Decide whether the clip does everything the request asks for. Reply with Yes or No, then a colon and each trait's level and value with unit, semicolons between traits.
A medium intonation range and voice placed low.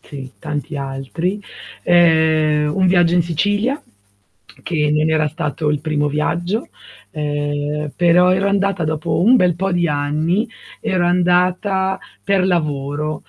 No: average, 3.4 semitones; medium, 165 Hz